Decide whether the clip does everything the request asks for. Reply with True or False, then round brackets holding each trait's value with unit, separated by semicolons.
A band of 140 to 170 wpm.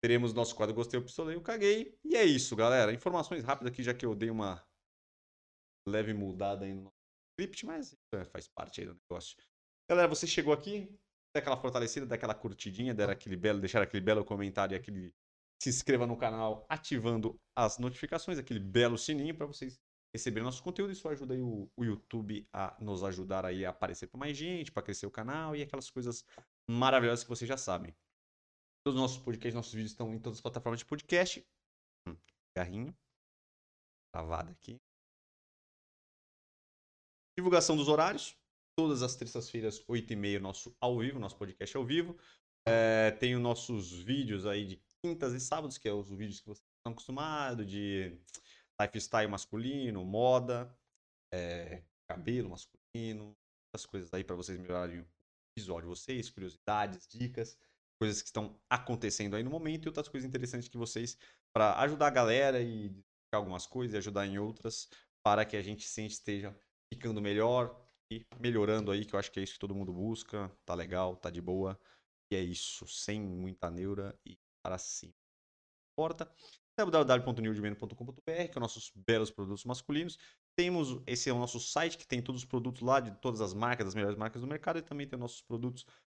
False (180 wpm)